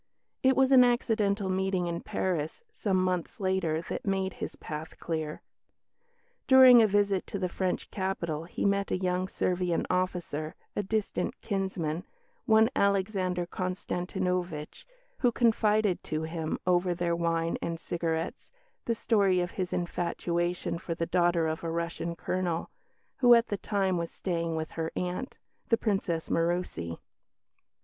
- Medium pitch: Yes, medium, 180 Hz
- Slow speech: No, average, 145 wpm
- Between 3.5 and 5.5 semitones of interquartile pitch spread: No, average, 2.9 semitones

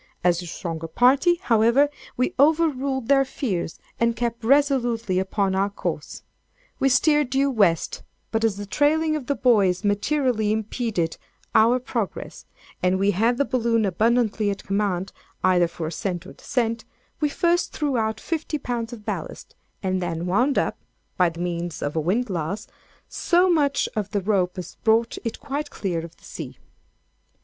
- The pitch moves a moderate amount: No, wide, 5.9 semitones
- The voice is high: Yes, high, 225 Hz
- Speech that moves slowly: No, average, 160 wpm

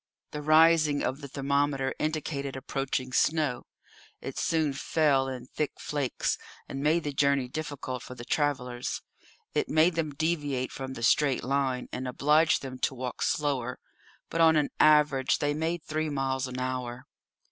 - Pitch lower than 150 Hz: Yes, medium, 140 Hz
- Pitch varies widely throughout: No, average, 2.8 semitones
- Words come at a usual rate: Yes, average, 160 wpm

